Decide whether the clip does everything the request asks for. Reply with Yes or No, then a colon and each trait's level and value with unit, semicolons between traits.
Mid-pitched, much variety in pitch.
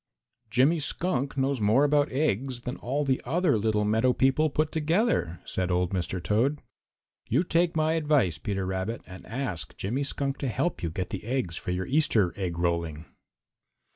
No: low, 125 Hz; wide, 7.7 semitones